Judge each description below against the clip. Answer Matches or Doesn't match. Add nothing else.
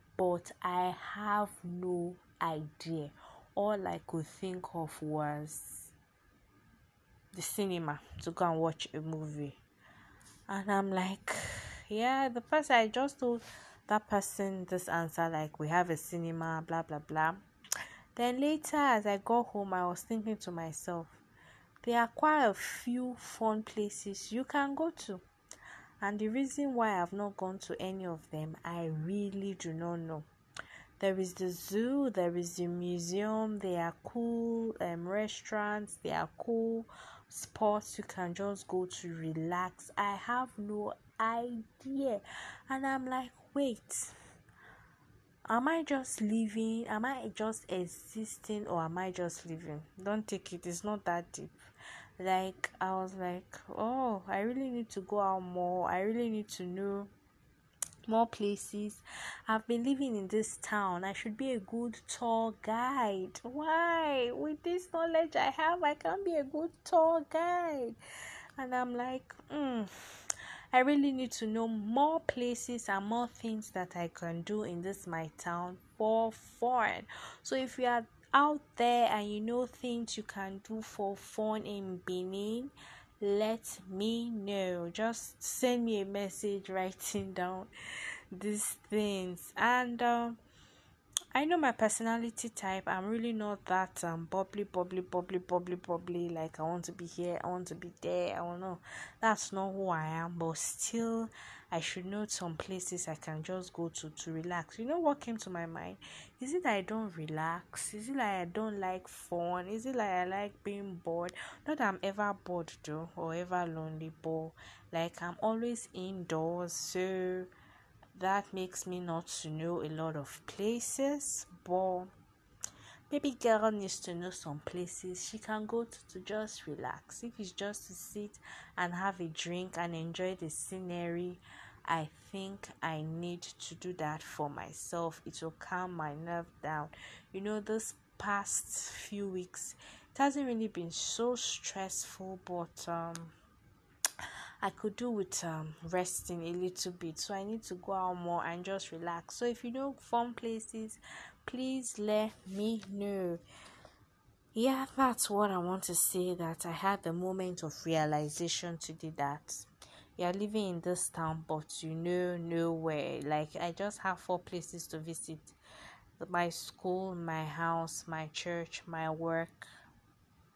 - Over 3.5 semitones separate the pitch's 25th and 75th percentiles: Matches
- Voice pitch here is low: Doesn't match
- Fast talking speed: Doesn't match